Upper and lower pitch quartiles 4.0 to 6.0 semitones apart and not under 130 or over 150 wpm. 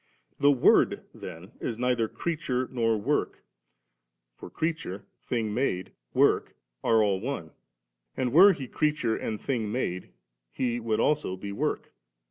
Yes: average, 4.6 semitones; average, 140 wpm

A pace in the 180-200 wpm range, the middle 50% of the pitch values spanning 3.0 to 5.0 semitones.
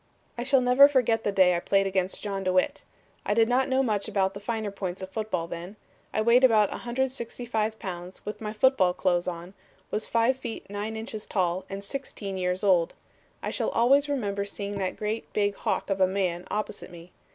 Yes: average, 195 wpm; average, 3.6 semitones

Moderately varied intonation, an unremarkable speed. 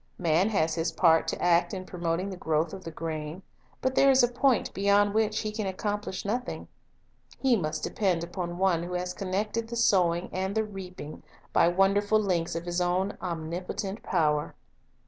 Yes: average, 3.3 semitones; average, 180 wpm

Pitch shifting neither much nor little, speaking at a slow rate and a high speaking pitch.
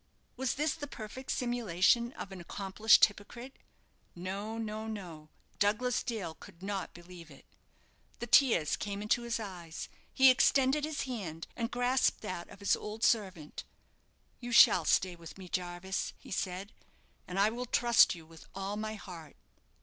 No: average, 4.9 semitones; average, 155 wpm; high, 205 Hz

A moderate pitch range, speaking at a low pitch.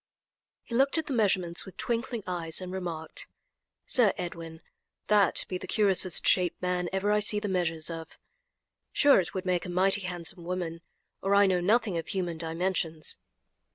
No: average, 3.0 semitones; medium, 185 Hz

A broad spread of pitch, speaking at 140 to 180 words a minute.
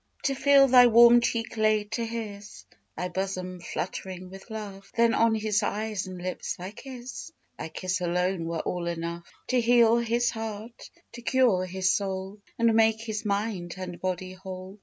No: average, 3.8 semitones; average, 170 wpm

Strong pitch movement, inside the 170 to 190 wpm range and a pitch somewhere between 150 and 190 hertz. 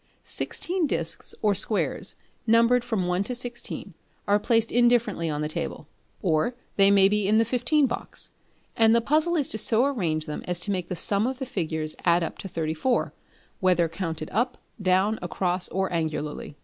No: wide, 5.7 semitones; average, 180 wpm; high, 200 Hz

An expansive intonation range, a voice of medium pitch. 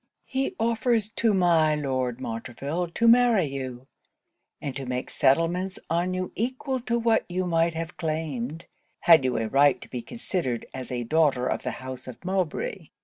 Yes: wide, 6.6 semitones; medium, 165 Hz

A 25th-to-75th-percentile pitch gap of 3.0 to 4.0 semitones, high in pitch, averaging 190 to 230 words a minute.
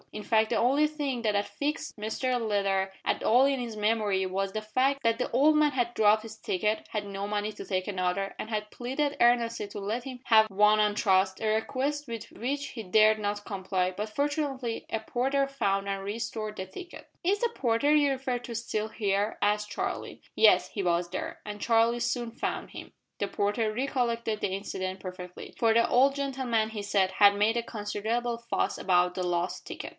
Yes: average, 3.4 semitones; high, 220 Hz; average, 200 wpm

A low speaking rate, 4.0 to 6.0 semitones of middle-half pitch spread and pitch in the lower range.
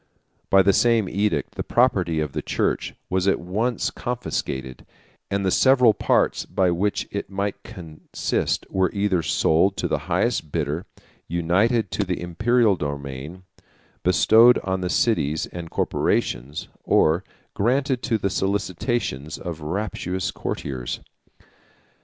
Yes: slow, 130 wpm; average, 4.6 semitones; very low, 95 Hz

